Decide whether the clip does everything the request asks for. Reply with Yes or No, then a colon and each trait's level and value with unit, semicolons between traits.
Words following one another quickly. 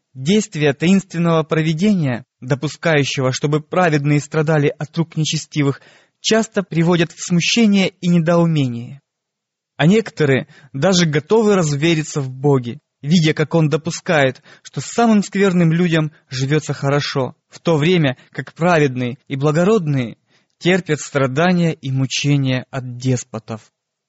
No: average, 115 wpm